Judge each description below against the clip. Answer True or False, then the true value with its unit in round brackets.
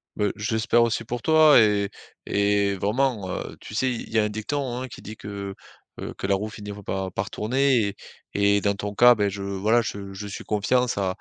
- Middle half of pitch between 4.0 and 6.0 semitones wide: False (2.9 semitones)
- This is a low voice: True (105 Hz)